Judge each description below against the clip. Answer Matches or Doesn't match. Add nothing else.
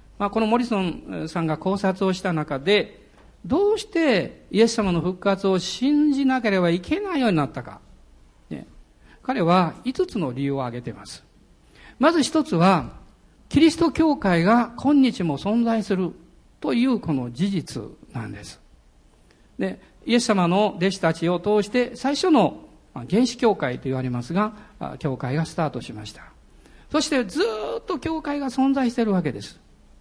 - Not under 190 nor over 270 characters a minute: Doesn't match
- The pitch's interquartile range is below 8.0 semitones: Doesn't match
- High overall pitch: Matches